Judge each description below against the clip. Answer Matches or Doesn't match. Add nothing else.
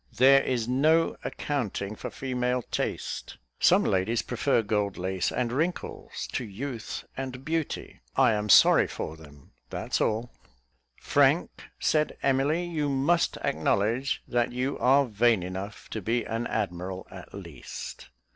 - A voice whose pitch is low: Matches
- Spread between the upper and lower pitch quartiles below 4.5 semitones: Doesn't match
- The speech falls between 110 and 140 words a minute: Matches